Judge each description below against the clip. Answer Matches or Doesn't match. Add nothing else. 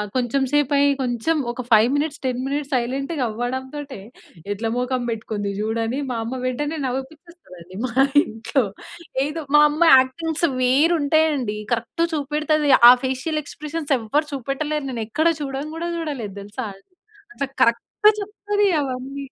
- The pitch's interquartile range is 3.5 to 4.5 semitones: Matches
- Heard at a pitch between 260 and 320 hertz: Matches